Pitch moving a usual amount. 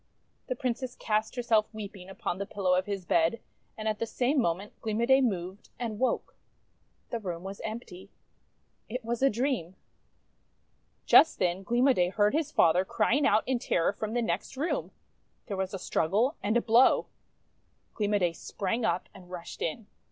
Yes: average, 4.3 semitones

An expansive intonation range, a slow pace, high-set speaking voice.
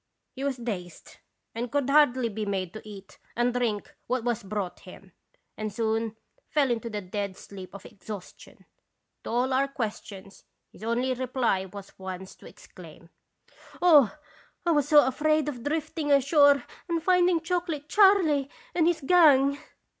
No: wide, 5.9 semitones; average, 155 wpm; very high, 250 Hz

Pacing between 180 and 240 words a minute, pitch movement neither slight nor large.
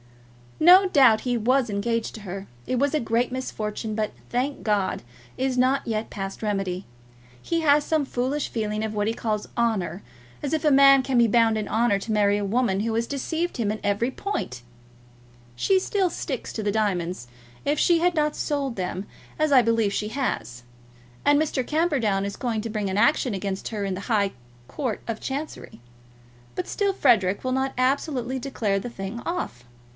Yes: average, 190 wpm; average, 5.0 semitones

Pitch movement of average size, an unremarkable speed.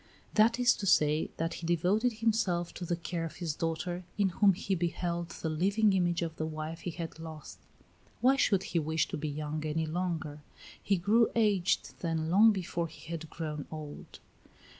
Yes: average, 3.5 semitones; average, 185 wpm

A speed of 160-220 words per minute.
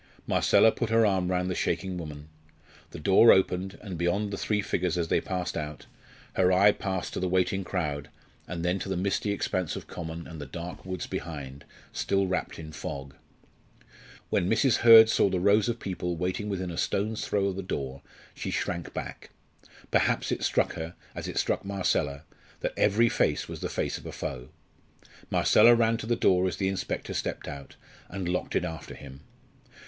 Yes: average, 190 wpm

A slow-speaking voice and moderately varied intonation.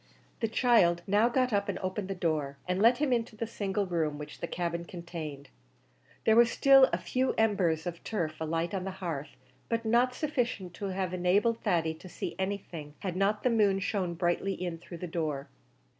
No: average, 195 wpm; average, 4.6 semitones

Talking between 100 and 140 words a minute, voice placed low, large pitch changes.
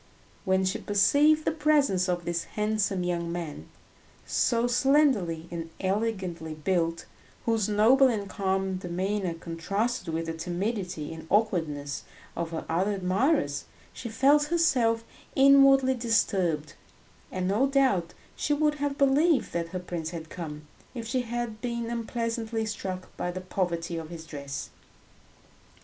No: slow, 135 wpm; high, 195 Hz; wide, 6.0 semitones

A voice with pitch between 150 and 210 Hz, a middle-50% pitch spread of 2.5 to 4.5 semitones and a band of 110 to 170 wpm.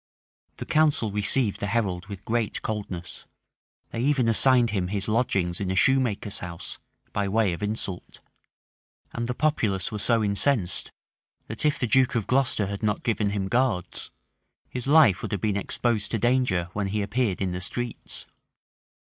No: low, 105 Hz; average, 3.9 semitones; average, 165 wpm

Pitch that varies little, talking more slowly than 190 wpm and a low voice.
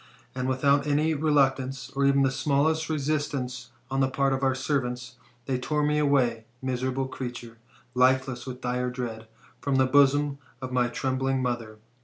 Yes: narrow, 1.9 semitones; average, 160 wpm; low, 130 Hz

